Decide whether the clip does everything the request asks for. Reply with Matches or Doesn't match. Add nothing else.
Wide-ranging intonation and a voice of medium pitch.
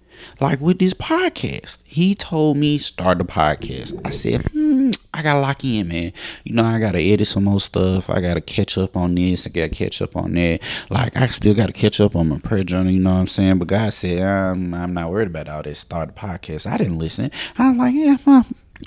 Doesn't match